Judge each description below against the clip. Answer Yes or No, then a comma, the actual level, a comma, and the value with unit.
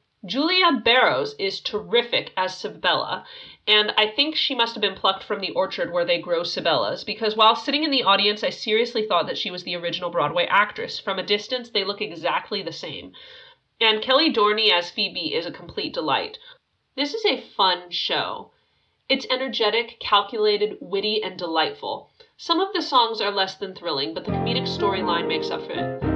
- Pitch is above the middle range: Yes, high, 220 Hz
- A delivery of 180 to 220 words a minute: Yes, average, 185 wpm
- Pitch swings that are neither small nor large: No, wide, 7.7 semitones